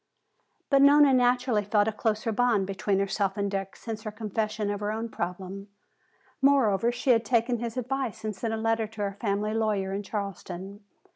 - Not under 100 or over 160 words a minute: No, average, 185 wpm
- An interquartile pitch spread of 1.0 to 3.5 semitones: Yes, average, 2.7 semitones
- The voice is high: Yes, high, 215 Hz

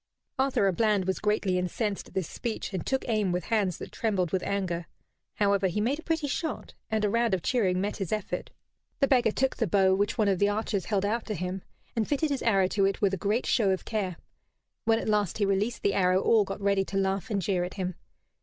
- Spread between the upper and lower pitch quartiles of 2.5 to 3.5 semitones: Yes, average, 2.8 semitones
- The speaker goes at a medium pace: No, fast, 240 wpm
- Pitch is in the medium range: No, high, 200 Hz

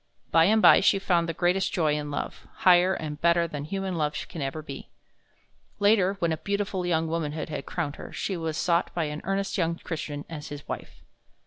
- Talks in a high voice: No, medium, 170 Hz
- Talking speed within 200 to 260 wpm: Yes, fast, 205 wpm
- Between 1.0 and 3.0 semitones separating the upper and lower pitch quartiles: No, average, 3.5 semitones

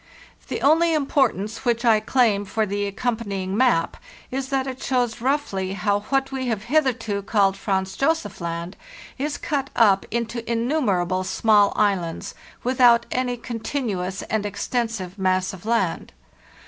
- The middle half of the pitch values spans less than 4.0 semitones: No, average, 4.7 semitones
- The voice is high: Yes, high, 225 Hz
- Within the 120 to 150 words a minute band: Yes, average, 140 wpm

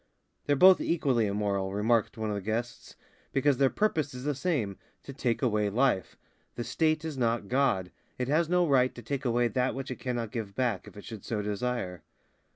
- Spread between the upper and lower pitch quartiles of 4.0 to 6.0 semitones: Yes, average, 4.6 semitones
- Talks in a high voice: No, low, 125 Hz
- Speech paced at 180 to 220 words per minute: Yes, average, 200 wpm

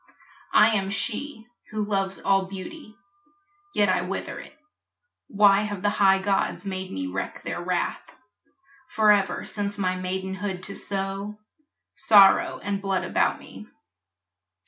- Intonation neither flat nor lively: No, narrow, 1.4 semitones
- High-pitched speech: Yes, high, 195 Hz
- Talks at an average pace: No, slow, 130 wpm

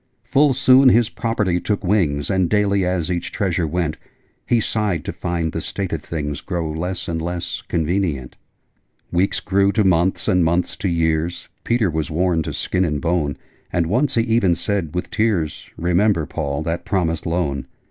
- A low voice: Yes, very low, 90 Hz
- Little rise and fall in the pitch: No, average, 3.5 semitones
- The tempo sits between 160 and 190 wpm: Yes, average, 175 wpm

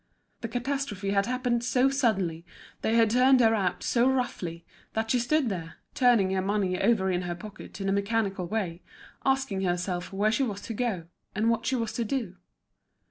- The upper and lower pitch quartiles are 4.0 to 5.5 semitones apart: Yes, average, 4.3 semitones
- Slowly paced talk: No, average, 190 wpm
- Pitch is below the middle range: No, high, 215 Hz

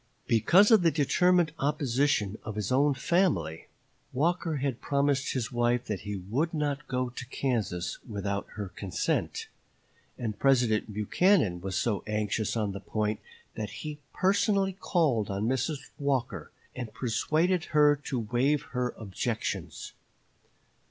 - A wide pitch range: Yes, wide, 5.8 semitones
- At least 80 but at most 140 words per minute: Yes, slow, 135 wpm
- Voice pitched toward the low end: Yes, low, 125 Hz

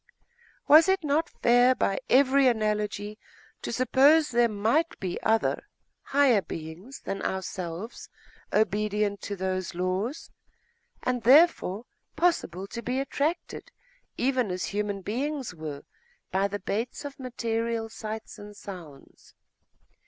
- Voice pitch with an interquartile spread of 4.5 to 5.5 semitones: Yes, average, 5.0 semitones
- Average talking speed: No, slow, 125 wpm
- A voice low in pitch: No, high, 220 Hz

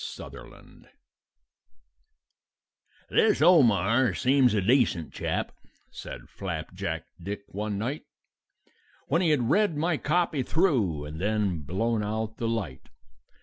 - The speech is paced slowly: Yes, slow, 110 wpm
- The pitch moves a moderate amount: No, wide, 6.3 semitones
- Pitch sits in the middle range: No, low, 115 Hz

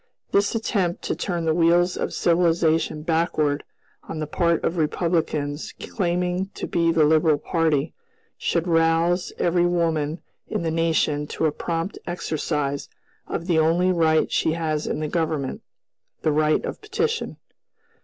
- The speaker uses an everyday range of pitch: No, narrow, 2.0 semitones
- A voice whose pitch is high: No, medium, 165 Hz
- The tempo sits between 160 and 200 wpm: No, average, 145 wpm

